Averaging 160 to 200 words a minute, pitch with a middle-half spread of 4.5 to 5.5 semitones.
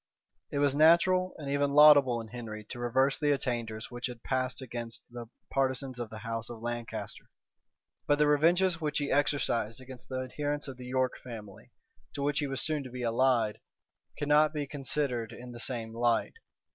No: average, 185 wpm; average, 3.5 semitones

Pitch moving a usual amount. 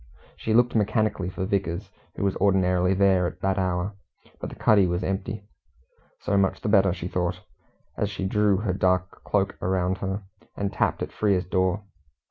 No: narrow, 1.8 semitones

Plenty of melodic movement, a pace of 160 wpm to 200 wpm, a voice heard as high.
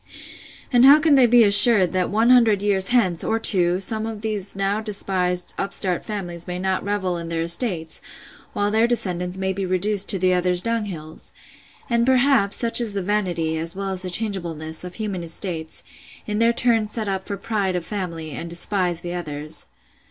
No: average, 3.5 semitones; average, 180 wpm; high, 195 Hz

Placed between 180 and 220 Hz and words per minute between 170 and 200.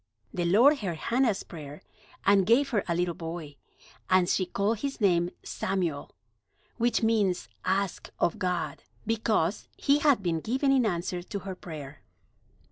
No: high, 190 Hz; average, 150 wpm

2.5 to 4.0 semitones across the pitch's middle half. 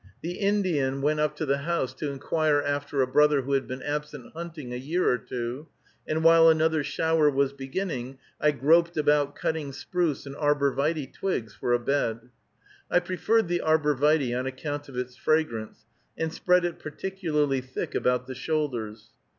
Yes: average, 3.4 semitones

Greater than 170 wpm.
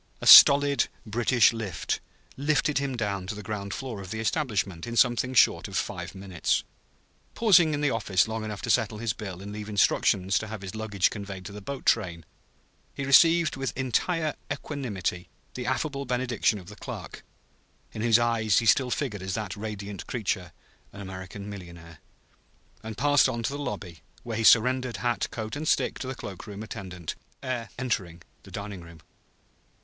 Yes: average, 180 wpm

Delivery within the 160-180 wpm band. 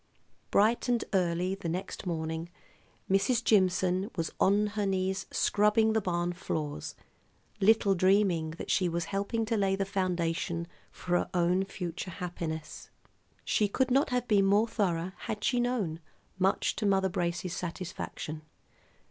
No: average, 145 wpm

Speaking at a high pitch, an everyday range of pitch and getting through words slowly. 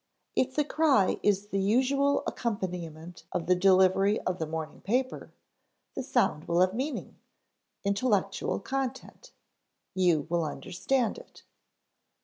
No: high, 195 Hz; wide, 6.3 semitones; slow, 125 wpm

